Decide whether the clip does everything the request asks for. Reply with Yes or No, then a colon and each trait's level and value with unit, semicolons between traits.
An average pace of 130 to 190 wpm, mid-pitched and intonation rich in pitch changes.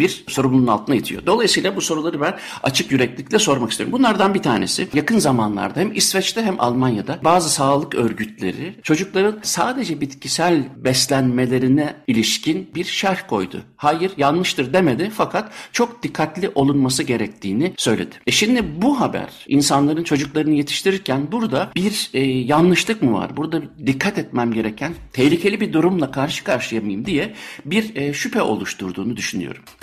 Yes: fast, 140 wpm; medium, 155 Hz; wide, 6.0 semitones